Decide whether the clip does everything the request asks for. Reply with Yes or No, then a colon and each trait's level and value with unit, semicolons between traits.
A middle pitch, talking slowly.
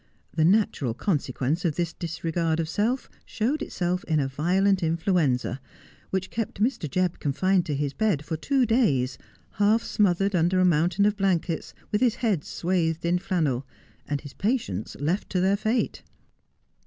No: medium, 175 Hz; average, 165 wpm